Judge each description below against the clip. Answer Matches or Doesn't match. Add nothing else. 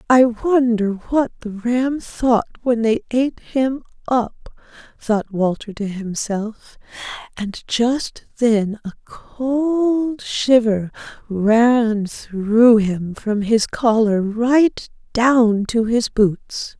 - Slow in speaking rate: Matches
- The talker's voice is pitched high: Matches